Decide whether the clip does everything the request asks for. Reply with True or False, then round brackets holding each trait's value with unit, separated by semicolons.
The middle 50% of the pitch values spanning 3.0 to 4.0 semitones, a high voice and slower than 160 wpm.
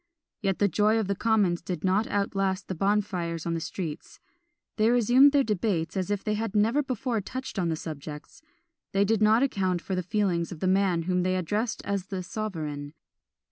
False (3.6 semitones; 195 Hz; 195 wpm)